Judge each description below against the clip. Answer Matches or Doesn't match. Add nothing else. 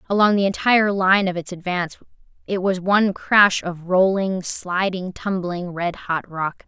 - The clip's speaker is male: Doesn't match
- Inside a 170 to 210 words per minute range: Doesn't match